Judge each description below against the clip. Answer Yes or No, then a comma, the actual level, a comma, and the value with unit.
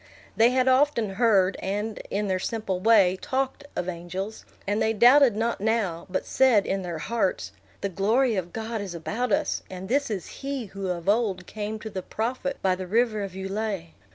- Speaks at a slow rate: No, average, 190 wpm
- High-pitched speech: Yes, high, 210 Hz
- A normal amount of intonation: Yes, average, 3.7 semitones